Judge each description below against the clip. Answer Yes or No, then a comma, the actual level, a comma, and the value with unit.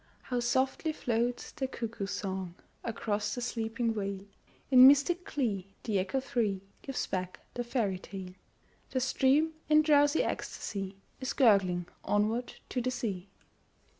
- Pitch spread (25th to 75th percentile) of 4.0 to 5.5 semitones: Yes, average, 4.9 semitones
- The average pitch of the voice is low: No, high, 230 Hz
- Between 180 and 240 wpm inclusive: No, slow, 135 wpm